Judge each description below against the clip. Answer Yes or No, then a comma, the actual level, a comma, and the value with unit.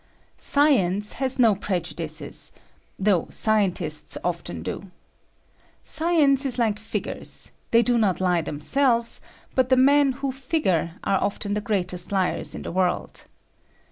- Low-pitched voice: No, high, 210 Hz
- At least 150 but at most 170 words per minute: No, slow, 135 wpm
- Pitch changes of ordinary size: No, wide, 6.4 semitones